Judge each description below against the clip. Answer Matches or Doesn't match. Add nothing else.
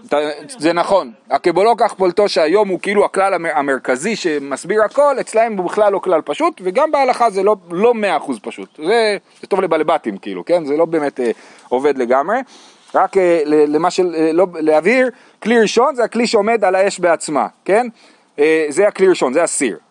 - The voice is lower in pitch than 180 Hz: Doesn't match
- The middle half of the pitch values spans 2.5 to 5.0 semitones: Doesn't match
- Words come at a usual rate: Doesn't match